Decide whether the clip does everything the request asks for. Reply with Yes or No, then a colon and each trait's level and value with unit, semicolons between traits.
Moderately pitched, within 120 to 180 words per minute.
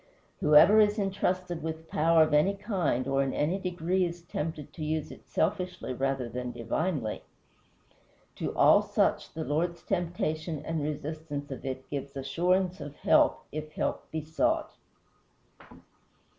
Yes: medium, 160 Hz; average, 145 wpm